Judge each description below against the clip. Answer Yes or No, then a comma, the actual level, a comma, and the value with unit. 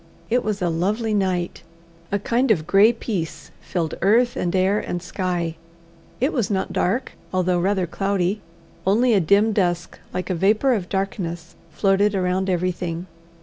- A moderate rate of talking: Yes, average, 155 wpm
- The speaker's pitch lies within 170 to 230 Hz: Yes, high, 190 Hz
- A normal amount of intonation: Yes, average, 3.0 semitones